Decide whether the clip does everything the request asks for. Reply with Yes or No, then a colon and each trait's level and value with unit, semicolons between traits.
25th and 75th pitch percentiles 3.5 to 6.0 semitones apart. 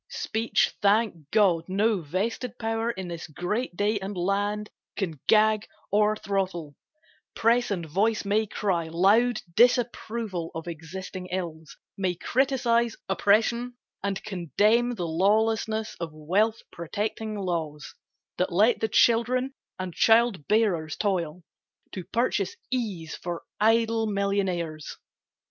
Yes: average, 4.3 semitones